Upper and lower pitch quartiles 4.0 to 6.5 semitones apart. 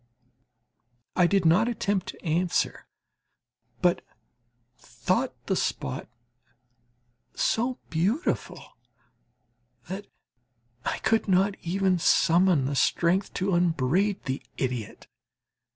No: average, 3.4 semitones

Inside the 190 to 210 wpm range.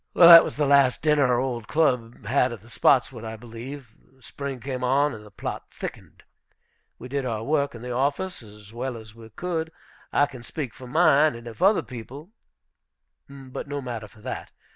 Yes: average, 195 wpm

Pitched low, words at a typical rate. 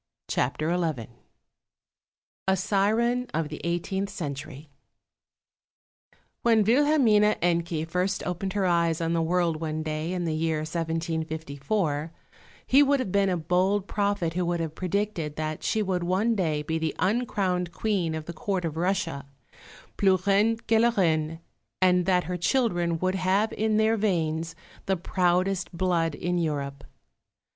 No: medium, 175 Hz; average, 150 wpm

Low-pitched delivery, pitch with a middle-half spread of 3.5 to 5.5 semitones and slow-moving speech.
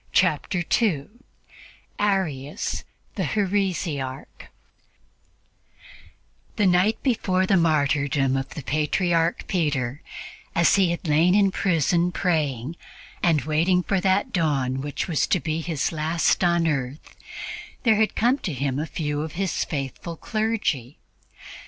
No: medium, 165 Hz; average, 4.5 semitones; slow, 125 wpm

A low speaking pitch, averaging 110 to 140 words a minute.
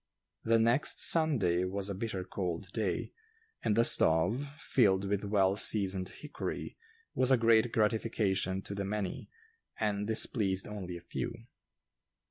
Yes: low, 100 Hz; slow, 135 wpm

